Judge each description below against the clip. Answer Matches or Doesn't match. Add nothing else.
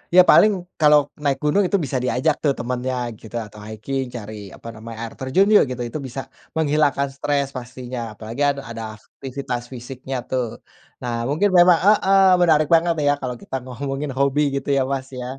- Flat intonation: Doesn't match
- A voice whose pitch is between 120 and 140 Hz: Matches